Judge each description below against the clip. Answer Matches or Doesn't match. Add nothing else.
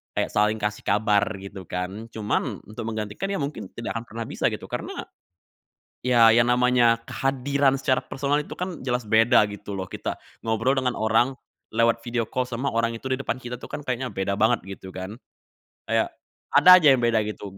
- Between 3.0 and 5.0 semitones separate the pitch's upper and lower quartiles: Matches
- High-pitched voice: Doesn't match